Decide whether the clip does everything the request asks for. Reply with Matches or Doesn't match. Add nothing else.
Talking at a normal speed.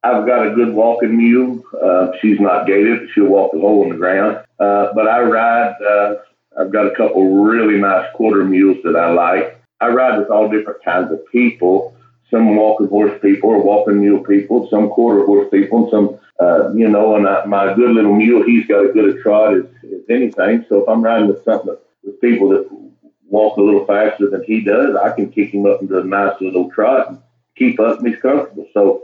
Doesn't match